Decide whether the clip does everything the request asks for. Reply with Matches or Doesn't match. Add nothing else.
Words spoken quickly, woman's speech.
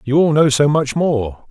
Doesn't match